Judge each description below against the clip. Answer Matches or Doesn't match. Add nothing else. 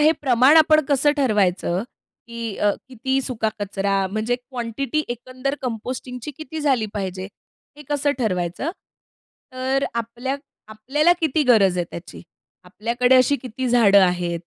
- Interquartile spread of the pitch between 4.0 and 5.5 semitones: Matches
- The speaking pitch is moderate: Doesn't match